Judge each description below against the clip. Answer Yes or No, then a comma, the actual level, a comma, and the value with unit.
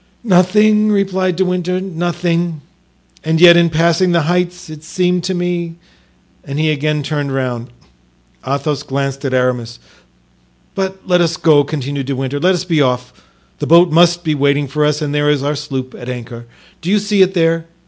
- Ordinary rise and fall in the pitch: Yes, average, 4.1 semitones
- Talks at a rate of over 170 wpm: Yes, average, 180 wpm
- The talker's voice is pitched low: No, medium, 160 Hz